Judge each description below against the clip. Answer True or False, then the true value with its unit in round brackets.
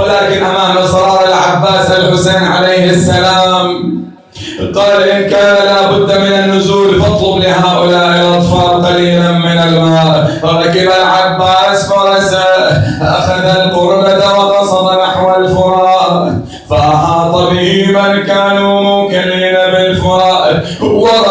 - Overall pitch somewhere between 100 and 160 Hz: False (185 Hz)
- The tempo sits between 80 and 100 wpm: True (85 wpm)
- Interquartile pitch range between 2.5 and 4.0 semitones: False (1.7 semitones)